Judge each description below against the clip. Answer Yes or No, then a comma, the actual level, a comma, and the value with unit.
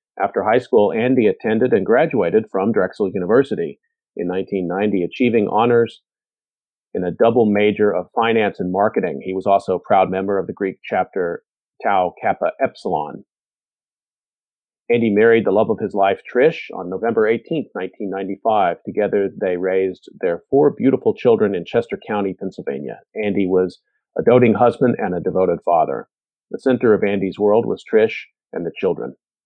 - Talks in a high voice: No, low, 105 Hz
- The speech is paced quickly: No, average, 155 wpm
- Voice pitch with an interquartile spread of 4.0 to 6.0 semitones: No, average, 3.6 semitones